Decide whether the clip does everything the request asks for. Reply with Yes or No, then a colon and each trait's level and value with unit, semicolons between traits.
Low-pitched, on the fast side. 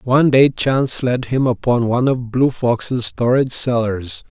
No: low, 125 Hz; average, 165 wpm